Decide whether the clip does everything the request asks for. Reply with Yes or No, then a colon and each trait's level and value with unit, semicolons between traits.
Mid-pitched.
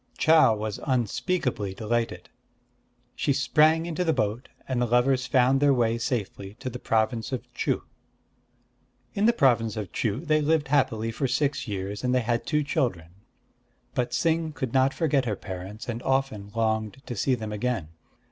No: low, 125 Hz